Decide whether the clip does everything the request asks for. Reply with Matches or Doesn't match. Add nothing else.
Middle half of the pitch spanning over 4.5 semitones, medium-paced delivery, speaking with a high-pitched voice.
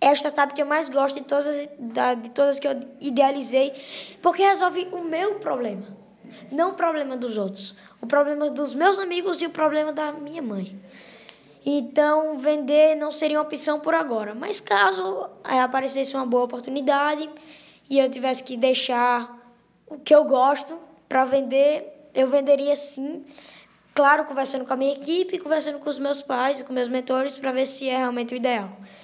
Doesn't match